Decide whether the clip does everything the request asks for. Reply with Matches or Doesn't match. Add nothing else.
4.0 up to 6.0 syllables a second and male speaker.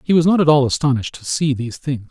Doesn't match